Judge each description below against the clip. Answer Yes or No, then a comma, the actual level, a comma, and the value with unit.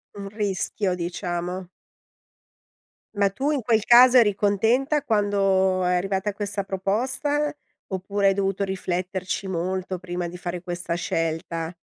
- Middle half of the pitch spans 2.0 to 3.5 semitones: Yes, narrow, 2.4 semitones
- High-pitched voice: Yes, high, 195 Hz